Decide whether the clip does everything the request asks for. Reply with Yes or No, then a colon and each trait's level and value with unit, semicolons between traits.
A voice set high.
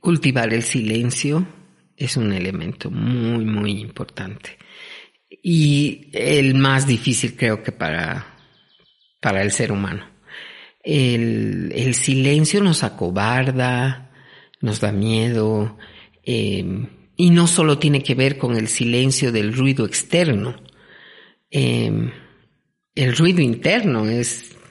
No: low, 125 Hz